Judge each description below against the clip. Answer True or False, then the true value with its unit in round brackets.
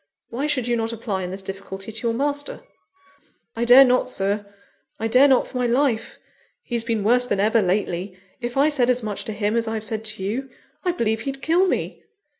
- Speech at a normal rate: False (215 wpm)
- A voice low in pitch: False (230 Hz)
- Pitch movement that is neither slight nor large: True (3.4 semitones)